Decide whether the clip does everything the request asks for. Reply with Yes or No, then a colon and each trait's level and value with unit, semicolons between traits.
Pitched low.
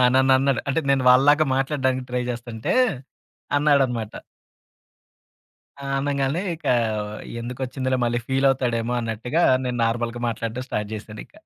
Yes: low, 130 Hz